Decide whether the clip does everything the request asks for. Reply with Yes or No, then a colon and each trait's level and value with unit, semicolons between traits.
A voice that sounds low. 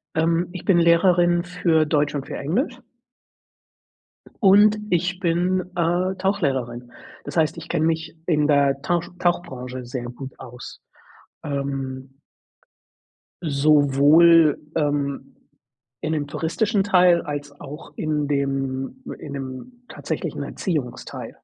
No: medium, 155 Hz